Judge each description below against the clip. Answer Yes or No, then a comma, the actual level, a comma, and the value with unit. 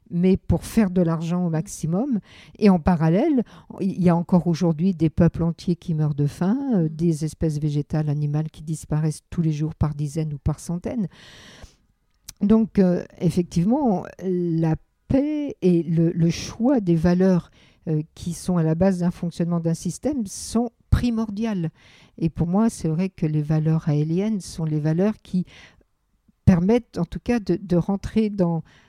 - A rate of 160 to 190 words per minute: Yes, average, 165 wpm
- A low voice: No, medium, 175 Hz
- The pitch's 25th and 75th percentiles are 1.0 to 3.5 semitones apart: Yes, average, 3.2 semitones